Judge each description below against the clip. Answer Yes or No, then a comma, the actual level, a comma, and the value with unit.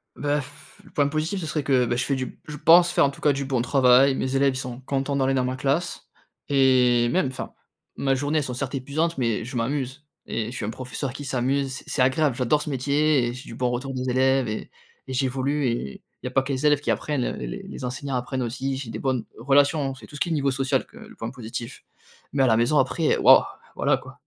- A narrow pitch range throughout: Yes, narrow, 2.3 semitones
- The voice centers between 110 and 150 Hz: Yes, low, 135 Hz